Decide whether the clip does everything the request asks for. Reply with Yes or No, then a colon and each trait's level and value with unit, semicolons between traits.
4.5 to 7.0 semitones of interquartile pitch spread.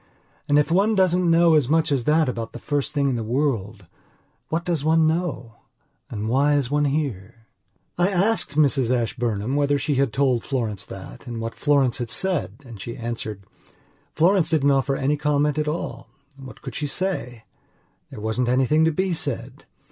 Yes: average, 4.8 semitones